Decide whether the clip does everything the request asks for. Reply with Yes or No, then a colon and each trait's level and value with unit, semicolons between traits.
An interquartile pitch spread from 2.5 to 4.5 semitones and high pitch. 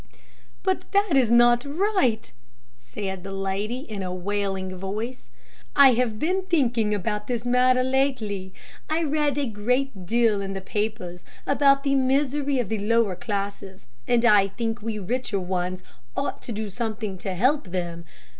No: average, 4.9 semitones; high, 225 Hz